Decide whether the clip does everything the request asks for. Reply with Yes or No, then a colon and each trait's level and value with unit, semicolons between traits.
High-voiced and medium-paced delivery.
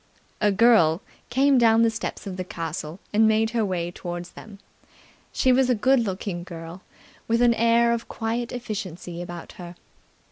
Yes: high, 215 Hz; average, 170 wpm